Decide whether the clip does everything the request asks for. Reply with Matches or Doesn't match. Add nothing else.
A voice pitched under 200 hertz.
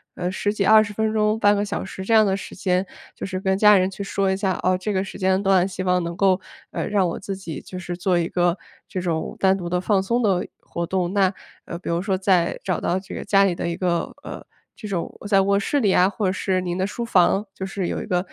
Matches